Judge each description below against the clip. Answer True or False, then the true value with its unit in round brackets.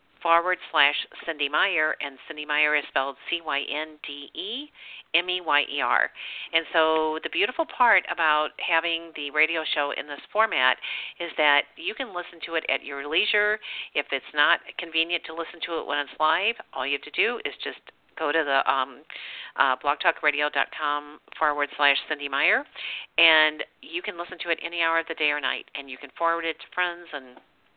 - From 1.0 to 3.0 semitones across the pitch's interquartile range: True (2.7 semitones)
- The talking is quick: False (195 wpm)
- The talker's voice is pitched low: False (155 Hz)